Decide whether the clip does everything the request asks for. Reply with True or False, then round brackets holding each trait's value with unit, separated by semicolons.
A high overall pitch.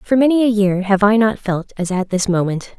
True (205 Hz)